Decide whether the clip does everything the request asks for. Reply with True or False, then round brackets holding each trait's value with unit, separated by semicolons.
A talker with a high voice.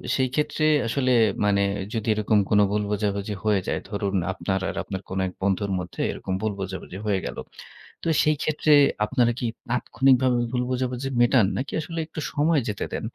False (110 Hz)